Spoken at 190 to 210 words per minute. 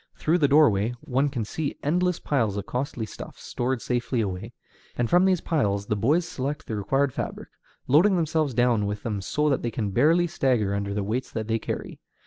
Yes: average, 200 wpm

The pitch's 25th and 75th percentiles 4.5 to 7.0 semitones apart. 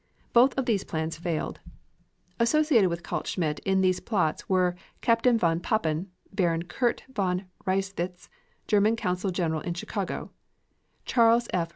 Yes: average, 4.8 semitones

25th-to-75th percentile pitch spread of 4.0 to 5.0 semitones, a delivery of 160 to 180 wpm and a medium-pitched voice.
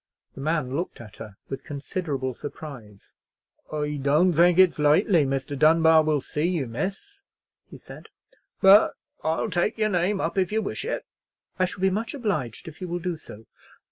Yes: average, 4.7 semitones; average, 175 wpm; medium, 160 Hz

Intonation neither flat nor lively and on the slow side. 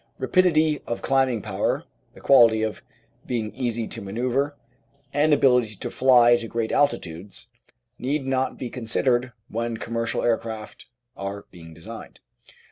Yes: average, 3.1 semitones; slow, 130 wpm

